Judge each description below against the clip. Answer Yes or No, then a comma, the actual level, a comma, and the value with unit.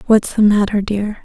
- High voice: Yes, high, 210 Hz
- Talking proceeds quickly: Yes, fast, 240 wpm